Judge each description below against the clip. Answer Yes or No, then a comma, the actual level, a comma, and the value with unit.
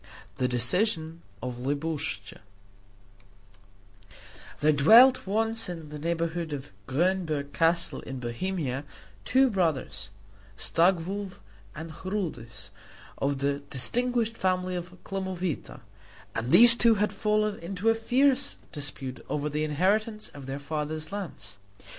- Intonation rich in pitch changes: Yes, wide, 6.1 semitones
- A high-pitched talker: No, medium, 170 Hz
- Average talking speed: No, slow, 115 wpm